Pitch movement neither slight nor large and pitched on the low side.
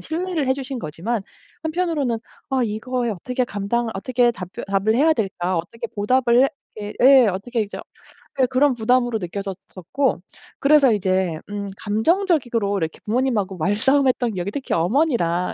No: average, 4.8 semitones; high, 235 Hz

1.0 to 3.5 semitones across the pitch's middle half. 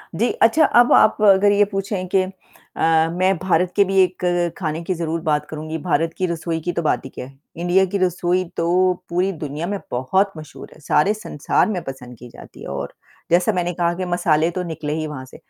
Yes: average, 3.0 semitones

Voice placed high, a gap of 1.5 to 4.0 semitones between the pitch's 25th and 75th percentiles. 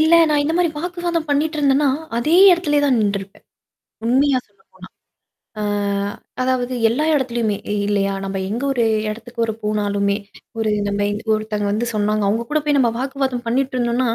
No: high, 245 Hz; average, 5.3 semitones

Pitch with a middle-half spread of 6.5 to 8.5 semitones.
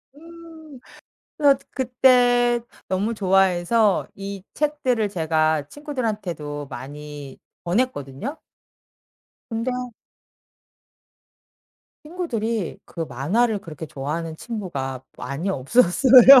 Yes: wide, 8.1 semitones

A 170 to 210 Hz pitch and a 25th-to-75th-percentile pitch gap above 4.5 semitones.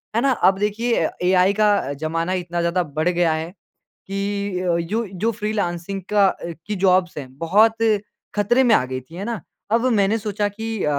No: high, 190 Hz; average, 3.7 semitones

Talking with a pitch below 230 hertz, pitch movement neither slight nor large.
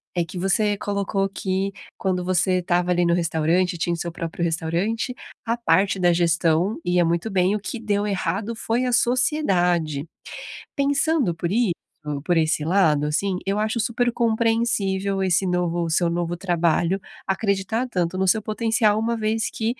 Yes: high, 190 Hz; average, 4.1 semitones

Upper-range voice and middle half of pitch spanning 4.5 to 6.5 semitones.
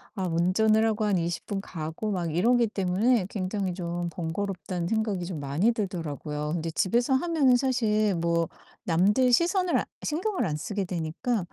Yes: high, 195 Hz; average, 4.9 semitones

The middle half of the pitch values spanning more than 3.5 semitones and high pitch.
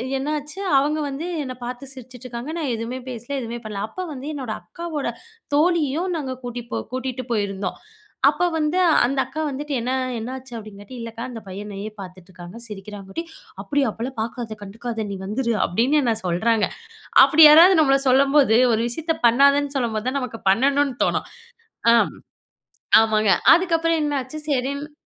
Yes: average, 4.5 semitones; very high, 255 Hz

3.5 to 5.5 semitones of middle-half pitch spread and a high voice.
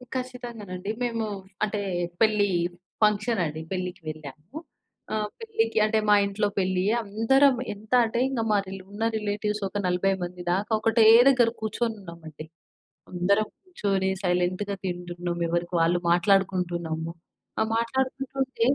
Yes: average, 4.0 semitones; high, 205 Hz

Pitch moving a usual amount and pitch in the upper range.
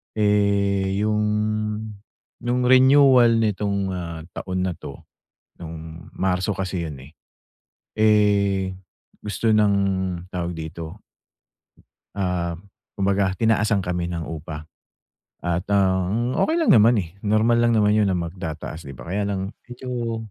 No: average, 3.6 semitones; low, 100 Hz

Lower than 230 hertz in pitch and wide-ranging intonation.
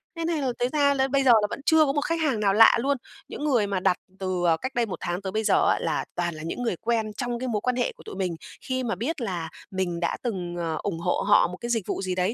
Yes: high, 220 Hz; wide, 6.1 semitones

